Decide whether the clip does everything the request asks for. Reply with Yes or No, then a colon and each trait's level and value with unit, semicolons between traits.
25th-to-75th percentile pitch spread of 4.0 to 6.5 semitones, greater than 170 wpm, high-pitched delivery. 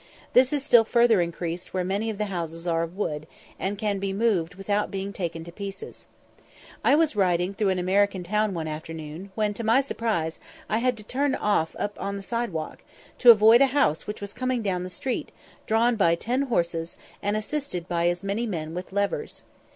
Yes: average, 4.4 semitones; average, 200 wpm; high, 200 Hz